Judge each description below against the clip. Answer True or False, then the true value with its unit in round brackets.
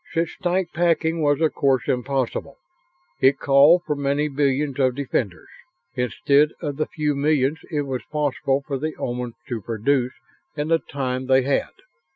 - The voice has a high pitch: False (140 Hz)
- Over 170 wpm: False (160 wpm)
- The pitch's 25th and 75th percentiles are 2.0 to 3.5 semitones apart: True (2.6 semitones)